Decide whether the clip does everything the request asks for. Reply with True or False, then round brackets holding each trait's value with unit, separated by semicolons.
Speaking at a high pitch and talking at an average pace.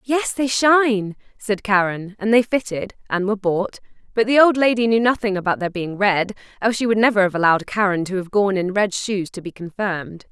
False (205 Hz; 215 wpm)